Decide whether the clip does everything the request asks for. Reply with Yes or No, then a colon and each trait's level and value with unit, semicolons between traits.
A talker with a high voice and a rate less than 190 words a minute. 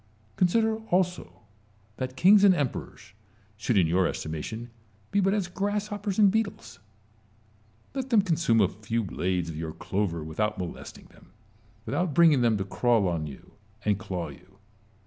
No: low, 115 Hz; average, 155 wpm